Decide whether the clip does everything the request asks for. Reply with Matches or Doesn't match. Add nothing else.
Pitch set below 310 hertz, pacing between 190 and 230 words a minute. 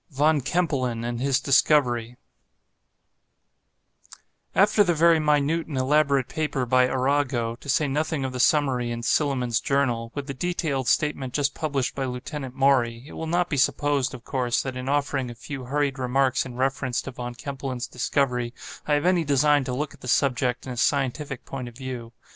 Doesn't match